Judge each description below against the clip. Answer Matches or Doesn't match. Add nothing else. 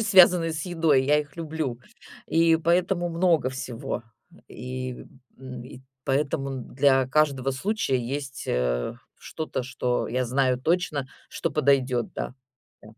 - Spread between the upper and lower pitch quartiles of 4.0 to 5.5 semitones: Matches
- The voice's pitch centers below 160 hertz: Matches